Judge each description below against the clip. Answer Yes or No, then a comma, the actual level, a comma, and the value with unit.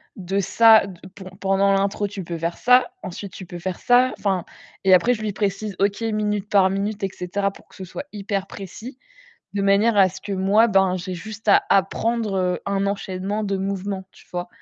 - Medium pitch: No, high, 195 Hz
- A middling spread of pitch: No, narrow, 1.8 semitones